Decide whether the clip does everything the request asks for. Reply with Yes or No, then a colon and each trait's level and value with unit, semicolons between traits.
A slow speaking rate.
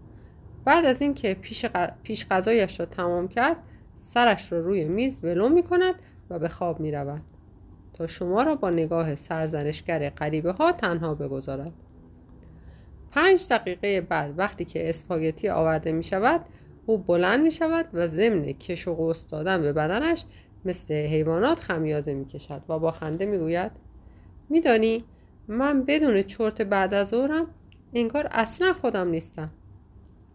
No: average, 145 wpm